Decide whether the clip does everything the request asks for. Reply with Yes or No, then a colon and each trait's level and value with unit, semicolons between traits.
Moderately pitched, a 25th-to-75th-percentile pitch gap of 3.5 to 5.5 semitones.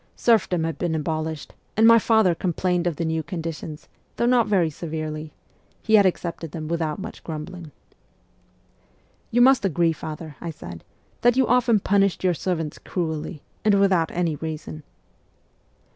Yes: medium, 170 Hz; average, 3.9 semitones